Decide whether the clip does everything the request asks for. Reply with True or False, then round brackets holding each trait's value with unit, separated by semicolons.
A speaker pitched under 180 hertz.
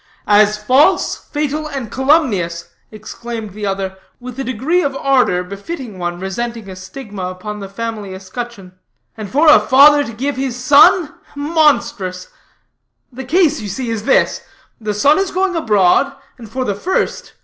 False (235 Hz)